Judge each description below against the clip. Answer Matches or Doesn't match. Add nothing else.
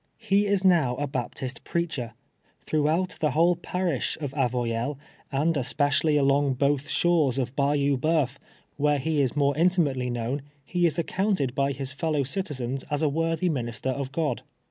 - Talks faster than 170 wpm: Doesn't match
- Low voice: Doesn't match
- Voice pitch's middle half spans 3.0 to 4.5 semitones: Matches